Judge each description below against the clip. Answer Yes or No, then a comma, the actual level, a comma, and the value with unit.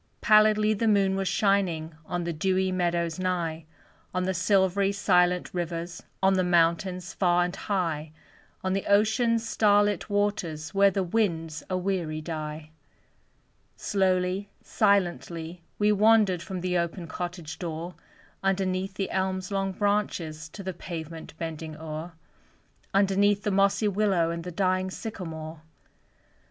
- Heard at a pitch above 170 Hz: Yes, medium, 185 Hz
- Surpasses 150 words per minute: No, slow, 135 wpm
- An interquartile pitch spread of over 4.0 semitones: No, average, 2.9 semitones